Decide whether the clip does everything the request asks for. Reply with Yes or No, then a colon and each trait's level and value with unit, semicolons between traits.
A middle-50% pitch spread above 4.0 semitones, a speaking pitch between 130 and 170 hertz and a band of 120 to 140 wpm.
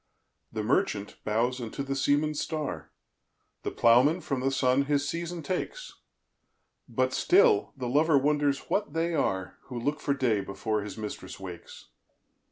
Yes: average, 5.2 semitones; medium, 140 Hz; slow, 135 wpm